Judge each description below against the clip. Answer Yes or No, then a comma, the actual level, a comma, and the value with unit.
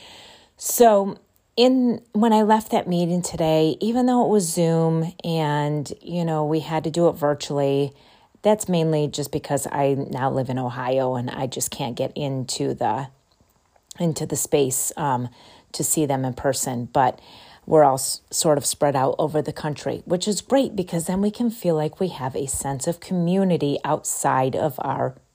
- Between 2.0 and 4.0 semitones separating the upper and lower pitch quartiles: No, average, 4.6 semitones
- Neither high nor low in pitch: Yes, medium, 155 Hz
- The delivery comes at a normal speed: Yes, average, 180 wpm